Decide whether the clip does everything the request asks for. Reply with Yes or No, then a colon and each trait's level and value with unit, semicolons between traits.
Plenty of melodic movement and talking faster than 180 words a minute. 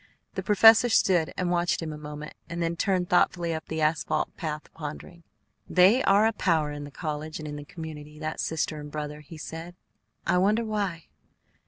No: average, 2.9 semitones; average, 190 wpm